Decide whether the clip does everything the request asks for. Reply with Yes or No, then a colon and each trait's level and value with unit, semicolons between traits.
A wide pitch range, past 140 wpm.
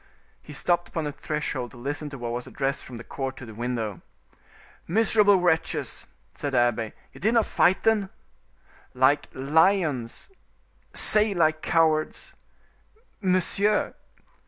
No: wide, 6.4 semitones; slow, 135 wpm